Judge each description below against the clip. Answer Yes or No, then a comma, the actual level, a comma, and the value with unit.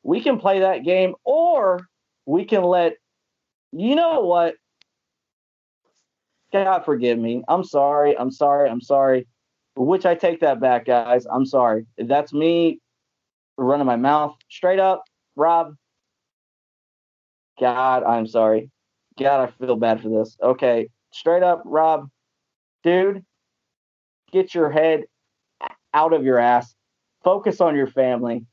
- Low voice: No, medium, 145 Hz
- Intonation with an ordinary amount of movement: No, wide, 6.2 semitones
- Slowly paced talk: Yes, slow, 130 wpm